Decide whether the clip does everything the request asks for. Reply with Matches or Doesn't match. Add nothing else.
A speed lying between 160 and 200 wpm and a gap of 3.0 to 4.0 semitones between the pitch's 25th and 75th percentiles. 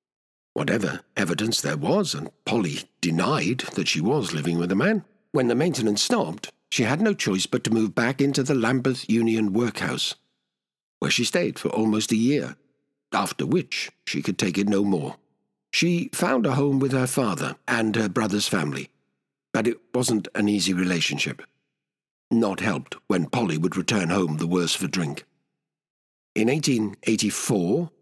Doesn't match